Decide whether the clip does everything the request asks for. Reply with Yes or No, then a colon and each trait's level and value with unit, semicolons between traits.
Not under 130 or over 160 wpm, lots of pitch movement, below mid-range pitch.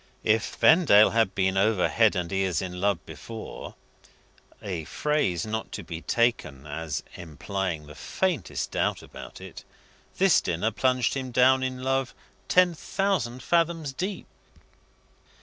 Yes: slow, 135 wpm; wide, 6.4 semitones; low, 110 Hz